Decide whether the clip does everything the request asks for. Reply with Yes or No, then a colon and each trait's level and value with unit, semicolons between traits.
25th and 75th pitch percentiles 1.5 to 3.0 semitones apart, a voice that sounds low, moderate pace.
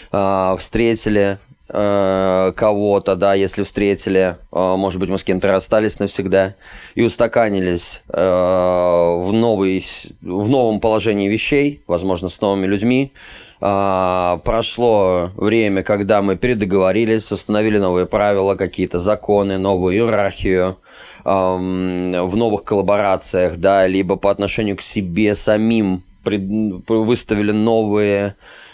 No: narrow, 2.4 semitones; low, 100 Hz; slow, 100 wpm